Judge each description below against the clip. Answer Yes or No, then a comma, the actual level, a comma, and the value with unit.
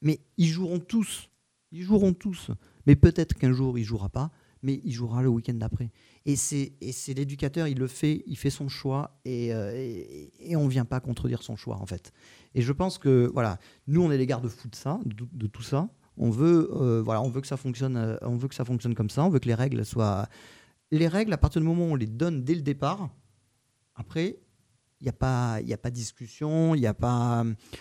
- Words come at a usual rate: No, fast, 235 wpm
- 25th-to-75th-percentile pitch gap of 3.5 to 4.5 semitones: Yes, average, 3.9 semitones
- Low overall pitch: Yes, low, 130 Hz